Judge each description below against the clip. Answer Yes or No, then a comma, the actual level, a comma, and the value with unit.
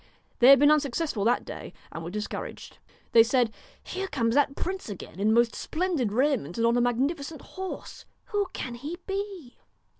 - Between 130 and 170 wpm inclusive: No, average, 185 wpm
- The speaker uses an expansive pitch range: Yes, wide, 6.1 semitones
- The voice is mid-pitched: No, very high, 265 Hz